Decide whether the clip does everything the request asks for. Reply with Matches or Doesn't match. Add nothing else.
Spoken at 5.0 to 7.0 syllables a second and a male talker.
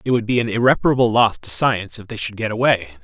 Matches